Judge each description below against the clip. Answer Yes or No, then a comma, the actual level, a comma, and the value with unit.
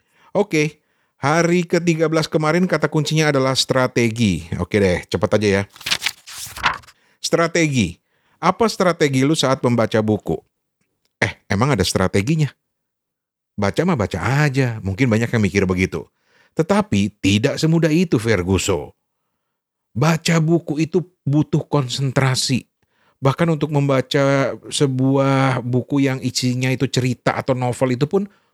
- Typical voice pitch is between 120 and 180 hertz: Yes, low, 135 Hz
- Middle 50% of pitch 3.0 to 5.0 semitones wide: No, wide, 5.5 semitones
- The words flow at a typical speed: Yes, average, 120 wpm